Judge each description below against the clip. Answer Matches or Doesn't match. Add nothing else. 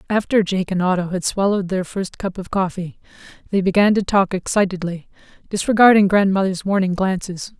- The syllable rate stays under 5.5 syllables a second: Doesn't match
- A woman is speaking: Matches